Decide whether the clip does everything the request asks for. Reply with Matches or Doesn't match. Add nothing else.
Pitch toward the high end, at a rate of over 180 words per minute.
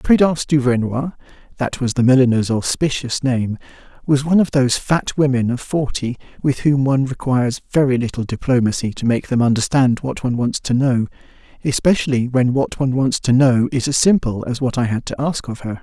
Doesn't match